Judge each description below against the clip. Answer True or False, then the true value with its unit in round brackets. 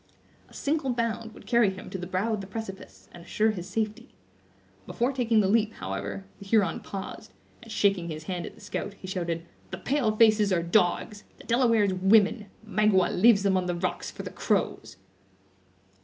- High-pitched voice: True (205 Hz)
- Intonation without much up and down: False (3.4 semitones)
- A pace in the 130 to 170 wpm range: False (185 wpm)